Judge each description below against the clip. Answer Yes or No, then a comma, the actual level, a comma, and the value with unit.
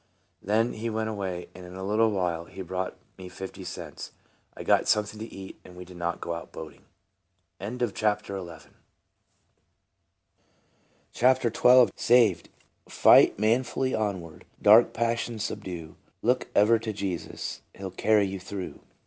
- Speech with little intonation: No, average, 3.6 semitones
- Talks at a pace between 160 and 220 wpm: No, average, 150 wpm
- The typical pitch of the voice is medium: No, low, 100 Hz